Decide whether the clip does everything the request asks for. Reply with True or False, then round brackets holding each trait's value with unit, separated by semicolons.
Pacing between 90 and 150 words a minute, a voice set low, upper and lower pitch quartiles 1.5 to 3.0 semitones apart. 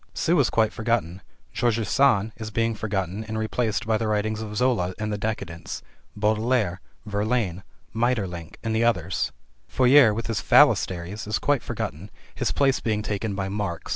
False (160 wpm; 110 Hz; 2.7 semitones)